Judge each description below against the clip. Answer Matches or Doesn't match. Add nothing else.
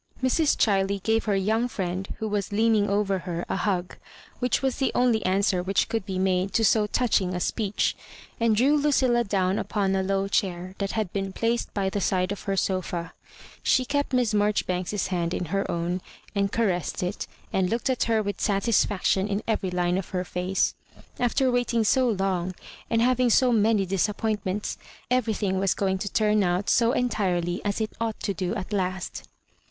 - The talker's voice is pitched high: Matches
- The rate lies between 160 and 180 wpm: Doesn't match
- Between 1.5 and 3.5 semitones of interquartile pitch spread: Matches